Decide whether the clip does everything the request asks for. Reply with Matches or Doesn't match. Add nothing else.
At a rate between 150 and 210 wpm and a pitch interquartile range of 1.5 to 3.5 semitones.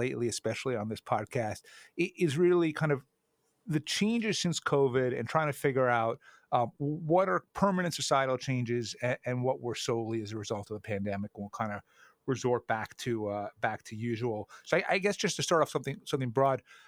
Doesn't match